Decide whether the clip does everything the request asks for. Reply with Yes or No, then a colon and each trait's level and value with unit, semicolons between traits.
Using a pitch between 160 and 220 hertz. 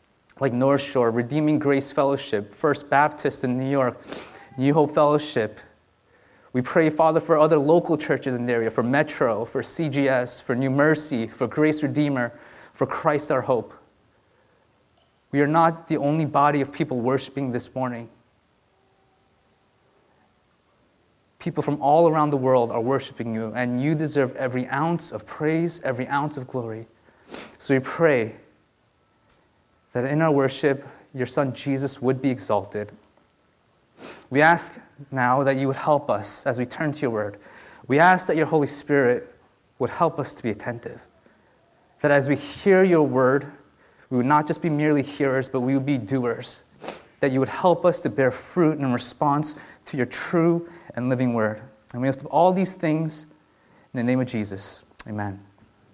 No: medium, 140 Hz